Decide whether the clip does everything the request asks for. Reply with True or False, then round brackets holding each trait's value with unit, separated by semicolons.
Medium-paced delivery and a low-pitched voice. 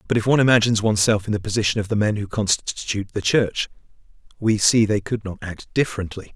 False (210 wpm; 105 Hz)